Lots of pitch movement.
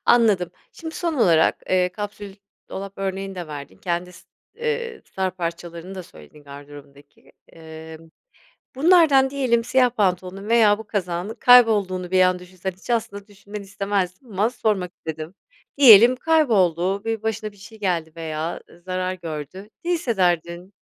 No: average, 4.4 semitones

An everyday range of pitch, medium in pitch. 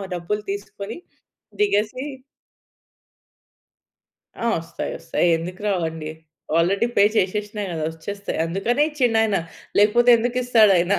No: average, 4.3 semitones; high, 205 Hz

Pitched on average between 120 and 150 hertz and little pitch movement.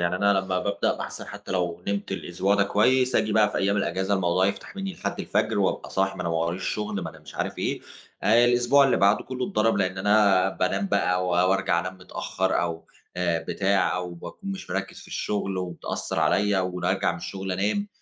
No: very low, 95 Hz; narrow, 2.3 semitones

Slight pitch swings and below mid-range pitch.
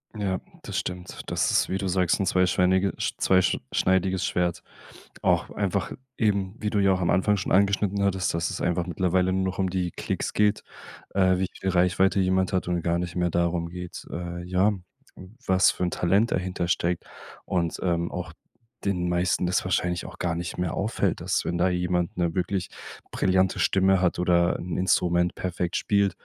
Yes: narrow, 1.3 semitones; very low, 90 Hz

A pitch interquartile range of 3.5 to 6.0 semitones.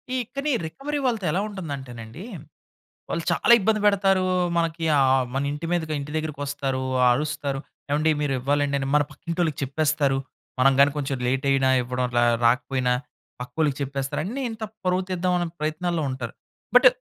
Yes: average, 4.5 semitones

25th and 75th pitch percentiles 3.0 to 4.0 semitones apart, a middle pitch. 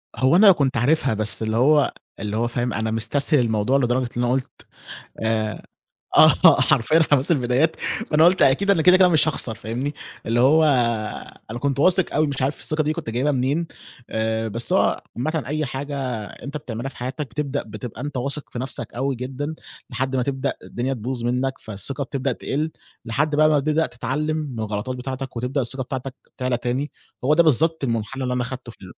No: average, 3.5 semitones; low, 130 Hz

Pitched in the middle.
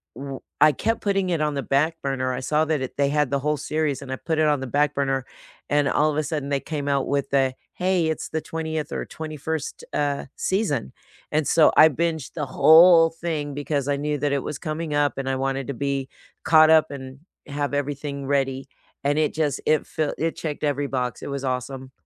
Yes: medium, 145 Hz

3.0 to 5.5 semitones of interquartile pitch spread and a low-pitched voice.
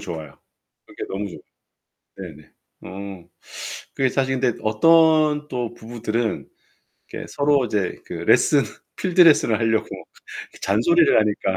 No: wide, 6.1 semitones; low, 120 Hz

